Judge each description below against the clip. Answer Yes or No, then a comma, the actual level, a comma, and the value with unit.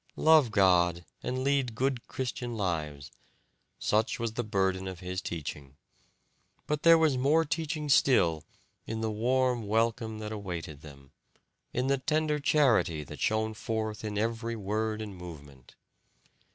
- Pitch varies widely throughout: Yes, wide, 5.9 semitones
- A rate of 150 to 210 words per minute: No, average, 140 wpm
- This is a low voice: Yes, low, 110 Hz